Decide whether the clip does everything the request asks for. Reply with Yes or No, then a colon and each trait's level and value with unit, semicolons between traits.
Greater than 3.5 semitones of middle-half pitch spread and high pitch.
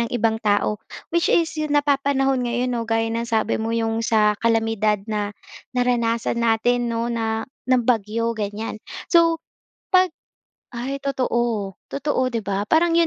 No: average, 3.0 semitones; high, 230 Hz